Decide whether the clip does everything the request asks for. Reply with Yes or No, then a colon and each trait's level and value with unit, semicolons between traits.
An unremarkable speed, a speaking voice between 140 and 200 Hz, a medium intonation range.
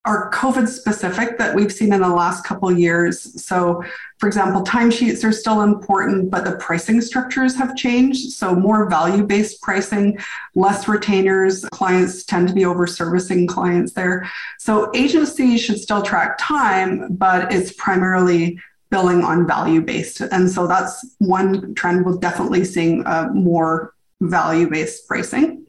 Yes: average, 155 wpm; high, 190 Hz; average, 3.3 semitones